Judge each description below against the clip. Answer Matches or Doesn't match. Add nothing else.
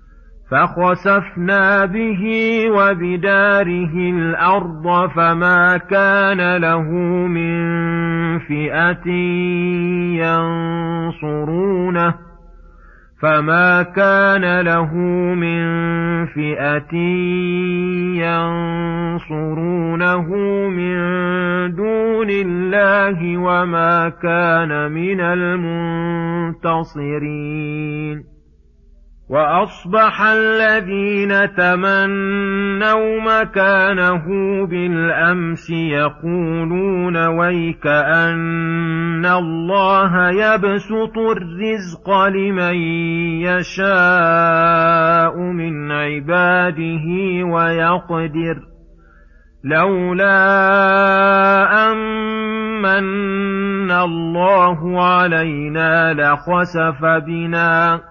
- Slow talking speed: Matches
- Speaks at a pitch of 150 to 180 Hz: Matches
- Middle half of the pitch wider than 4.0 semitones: Doesn't match